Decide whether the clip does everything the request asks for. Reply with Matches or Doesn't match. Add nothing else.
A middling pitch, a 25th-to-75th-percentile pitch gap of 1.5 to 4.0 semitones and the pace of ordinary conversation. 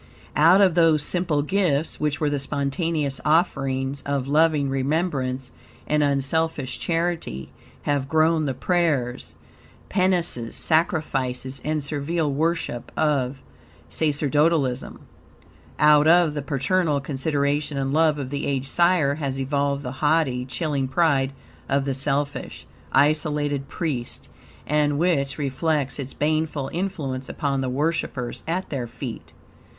Doesn't match